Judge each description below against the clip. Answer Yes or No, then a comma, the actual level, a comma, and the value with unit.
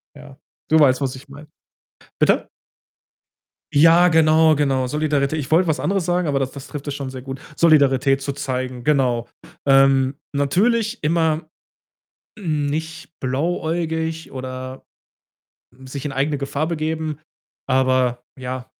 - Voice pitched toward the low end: No, medium, 145 Hz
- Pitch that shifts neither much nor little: Yes, average, 3.2 semitones